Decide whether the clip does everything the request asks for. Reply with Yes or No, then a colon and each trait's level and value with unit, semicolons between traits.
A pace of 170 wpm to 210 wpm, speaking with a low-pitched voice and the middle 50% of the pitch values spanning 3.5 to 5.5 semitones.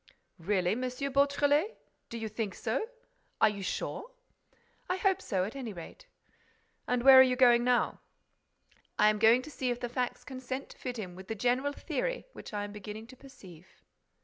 No: average, 180 wpm; high, 245 Hz; average, 4.4 semitones